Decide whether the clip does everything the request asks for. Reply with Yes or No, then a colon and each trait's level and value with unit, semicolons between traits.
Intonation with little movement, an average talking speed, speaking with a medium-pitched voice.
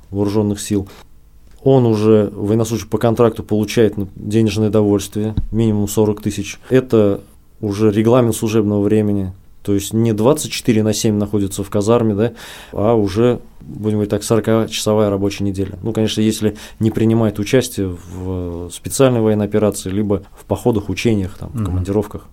No: narrow, 1.8 semitones; average, 140 wpm; low, 105 Hz